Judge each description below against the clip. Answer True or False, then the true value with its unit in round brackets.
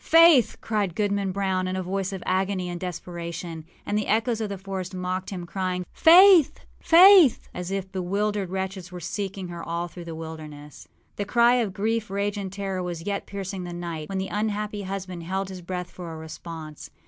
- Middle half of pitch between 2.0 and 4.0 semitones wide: True (2.6 semitones)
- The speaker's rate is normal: True (195 wpm)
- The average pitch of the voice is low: False (190 Hz)